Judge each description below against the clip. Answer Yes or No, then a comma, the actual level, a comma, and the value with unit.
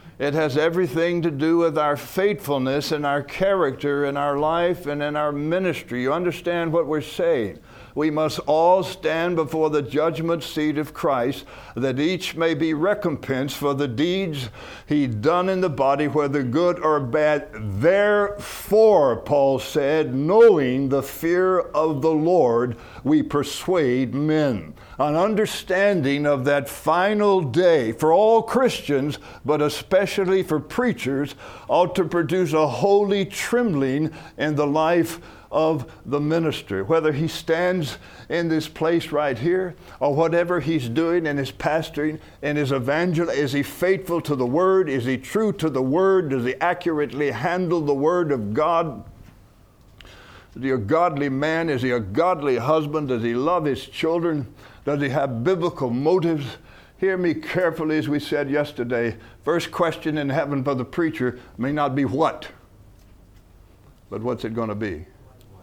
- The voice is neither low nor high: Yes, medium, 150 Hz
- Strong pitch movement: No, average, 3.8 semitones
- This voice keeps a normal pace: Yes, average, 155 wpm